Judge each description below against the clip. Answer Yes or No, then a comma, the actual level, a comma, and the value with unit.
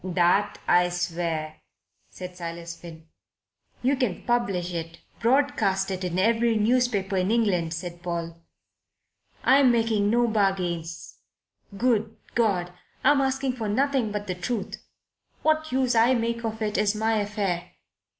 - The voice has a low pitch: No, high, 205 Hz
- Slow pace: Yes, slow, 130 wpm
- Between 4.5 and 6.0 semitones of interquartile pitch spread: Yes, average, 5.0 semitones